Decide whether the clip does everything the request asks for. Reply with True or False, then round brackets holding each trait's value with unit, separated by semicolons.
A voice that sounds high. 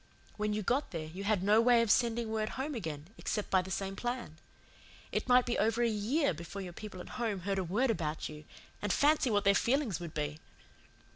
True (210 Hz)